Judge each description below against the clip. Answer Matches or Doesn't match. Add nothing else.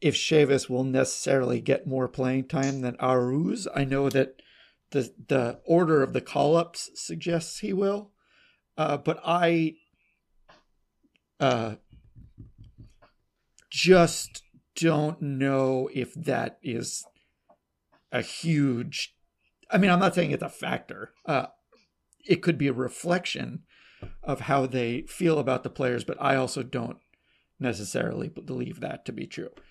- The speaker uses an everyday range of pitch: Matches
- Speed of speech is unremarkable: Doesn't match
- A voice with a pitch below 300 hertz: Matches